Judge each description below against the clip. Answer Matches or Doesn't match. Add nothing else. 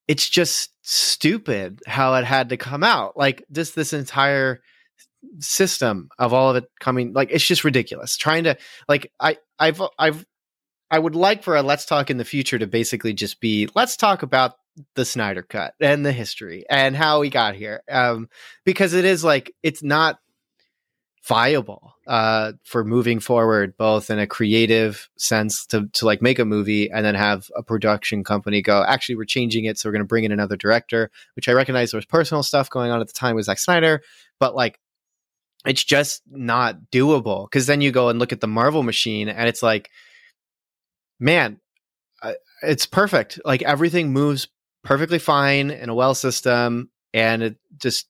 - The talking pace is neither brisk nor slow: Matches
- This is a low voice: Matches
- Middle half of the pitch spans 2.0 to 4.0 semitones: Doesn't match